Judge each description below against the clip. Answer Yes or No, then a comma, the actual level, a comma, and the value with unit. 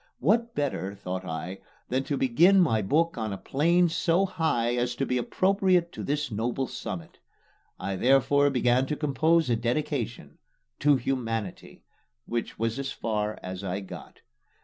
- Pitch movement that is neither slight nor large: No, wide, 5.9 semitones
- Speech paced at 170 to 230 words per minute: No, average, 150 wpm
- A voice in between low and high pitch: No, low, 130 Hz